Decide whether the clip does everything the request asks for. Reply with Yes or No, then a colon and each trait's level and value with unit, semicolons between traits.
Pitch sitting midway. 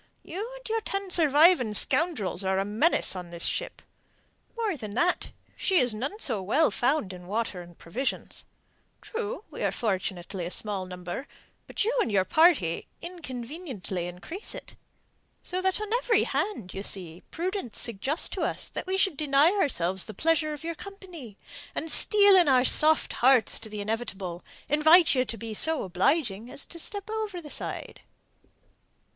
No: very high, 275 Hz